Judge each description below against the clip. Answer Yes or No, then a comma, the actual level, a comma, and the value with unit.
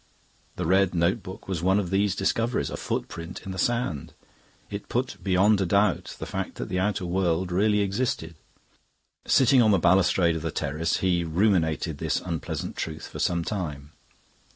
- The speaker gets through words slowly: No, average, 170 wpm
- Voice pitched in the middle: No, very low, 95 Hz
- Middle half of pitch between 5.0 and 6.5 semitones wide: No, average, 3.3 semitones